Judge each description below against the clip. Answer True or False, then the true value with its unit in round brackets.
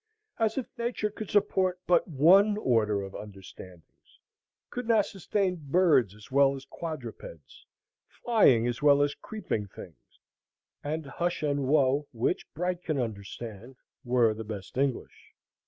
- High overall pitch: False (140 Hz)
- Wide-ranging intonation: True (8.0 semitones)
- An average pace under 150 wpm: True (140 wpm)